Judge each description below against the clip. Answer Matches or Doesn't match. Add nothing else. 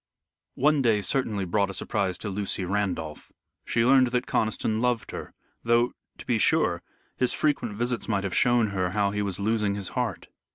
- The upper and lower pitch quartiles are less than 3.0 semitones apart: Doesn't match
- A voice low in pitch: Matches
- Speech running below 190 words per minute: Matches